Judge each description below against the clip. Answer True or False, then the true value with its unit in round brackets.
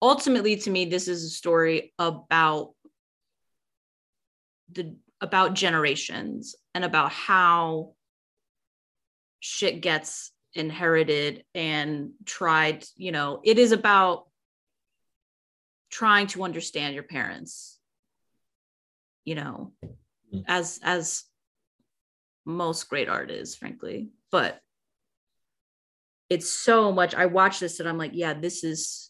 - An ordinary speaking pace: False (105 wpm)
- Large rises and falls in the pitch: False (3.9 semitones)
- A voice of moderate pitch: True (165 Hz)